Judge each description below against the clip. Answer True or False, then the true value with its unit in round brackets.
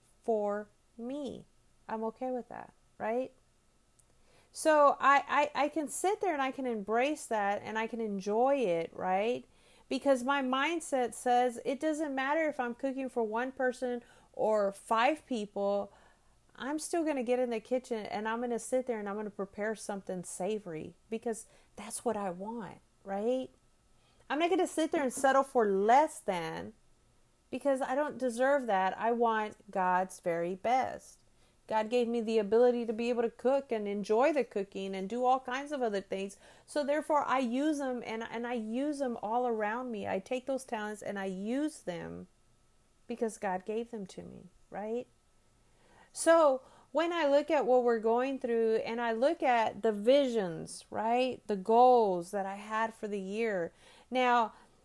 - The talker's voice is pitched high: True (235 Hz)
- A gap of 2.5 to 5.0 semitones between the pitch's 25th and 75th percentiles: True (4.0 semitones)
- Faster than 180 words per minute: False (175 wpm)